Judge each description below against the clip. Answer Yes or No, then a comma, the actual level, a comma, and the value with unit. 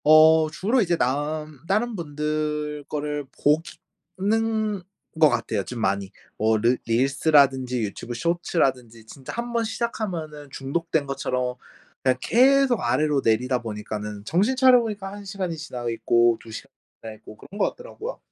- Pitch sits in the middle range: Yes, medium, 150 Hz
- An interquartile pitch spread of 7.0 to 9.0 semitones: Yes, wide, 7.6 semitones